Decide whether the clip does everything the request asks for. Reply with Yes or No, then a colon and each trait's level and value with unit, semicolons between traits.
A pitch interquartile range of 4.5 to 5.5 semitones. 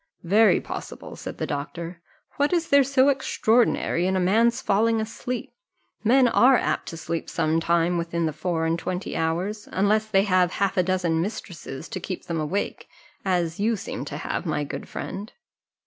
Yes: average, 4.8 semitones